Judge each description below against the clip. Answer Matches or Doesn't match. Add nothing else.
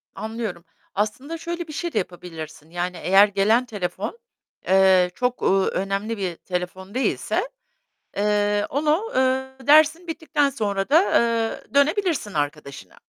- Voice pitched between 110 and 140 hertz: Doesn't match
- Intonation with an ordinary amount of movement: Doesn't match